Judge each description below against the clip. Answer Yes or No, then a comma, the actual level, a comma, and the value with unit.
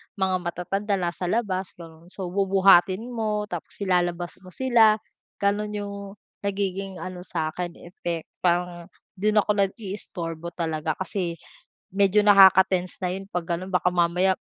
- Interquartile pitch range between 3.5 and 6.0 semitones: No, narrow, 2.4 semitones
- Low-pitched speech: No, medium, 185 Hz